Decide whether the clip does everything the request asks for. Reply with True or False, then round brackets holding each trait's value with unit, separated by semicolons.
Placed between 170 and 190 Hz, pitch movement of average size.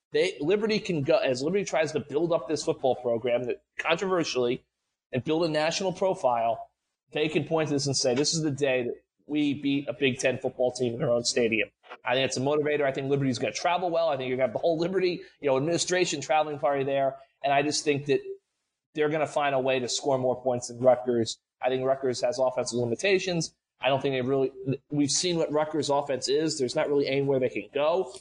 False (140 Hz; 3.6 semitones)